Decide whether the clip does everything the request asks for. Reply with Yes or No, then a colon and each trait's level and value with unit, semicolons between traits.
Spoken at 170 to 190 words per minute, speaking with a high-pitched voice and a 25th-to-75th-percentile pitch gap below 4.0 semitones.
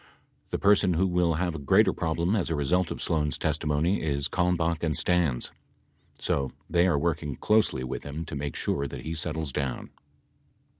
No: average, 180 wpm; very low, 80 Hz; average, 3.3 semitones